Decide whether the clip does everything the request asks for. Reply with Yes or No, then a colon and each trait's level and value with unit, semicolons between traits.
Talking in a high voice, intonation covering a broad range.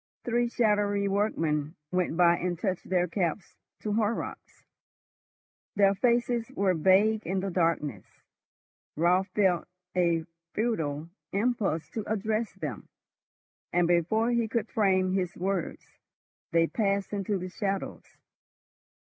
No: high, 195 Hz; average, 3.7 semitones